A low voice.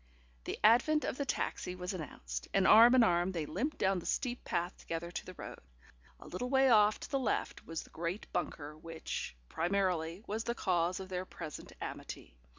No: medium, 185 Hz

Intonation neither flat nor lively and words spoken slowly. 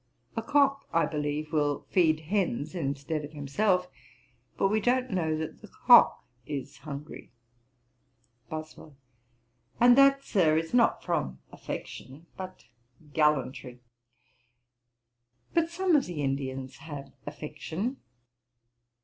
No: wide, 6.2 semitones; slow, 115 wpm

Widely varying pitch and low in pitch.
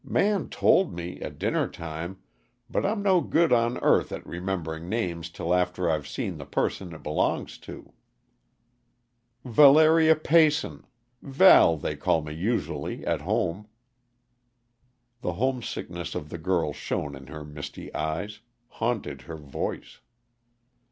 Yes: wide, 8.1 semitones; very low, 90 Hz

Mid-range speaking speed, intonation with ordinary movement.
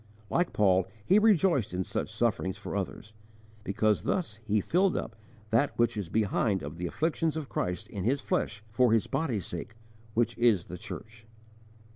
No: average, 170 wpm; wide, 5.7 semitones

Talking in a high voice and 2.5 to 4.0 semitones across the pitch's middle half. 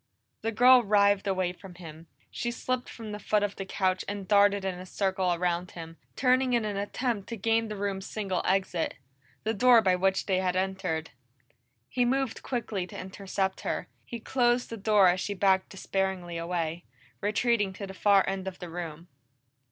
Yes: high, 195 Hz; average, 2.8 semitones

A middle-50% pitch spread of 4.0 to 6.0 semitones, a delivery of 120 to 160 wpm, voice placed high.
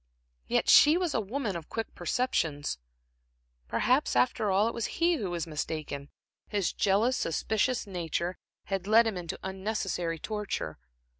Yes: average, 5.2 semitones; average, 145 wpm; high, 195 Hz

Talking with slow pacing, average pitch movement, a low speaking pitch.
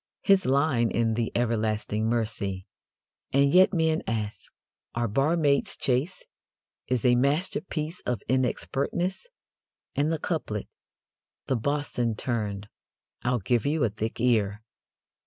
Yes: slow, 120 wpm; average, 4.9 semitones; low, 125 Hz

